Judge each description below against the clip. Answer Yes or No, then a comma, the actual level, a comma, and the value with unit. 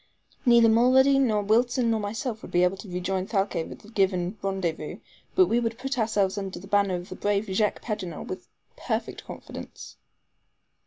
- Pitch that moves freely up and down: No, average, 3.3 semitones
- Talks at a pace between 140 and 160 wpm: No, average, 175 wpm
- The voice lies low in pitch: No, high, 205 Hz